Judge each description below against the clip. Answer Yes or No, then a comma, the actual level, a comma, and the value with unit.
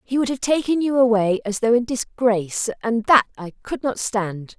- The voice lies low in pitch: No, high, 230 Hz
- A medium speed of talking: No, fast, 210 wpm